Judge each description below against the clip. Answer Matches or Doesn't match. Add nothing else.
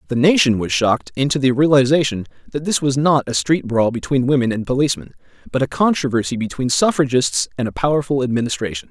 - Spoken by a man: Matches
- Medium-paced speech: Matches